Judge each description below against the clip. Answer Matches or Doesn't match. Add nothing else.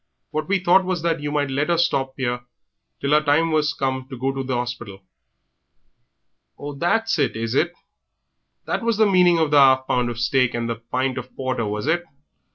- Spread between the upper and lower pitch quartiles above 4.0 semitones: Matches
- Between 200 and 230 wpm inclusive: Matches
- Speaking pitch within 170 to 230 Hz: Doesn't match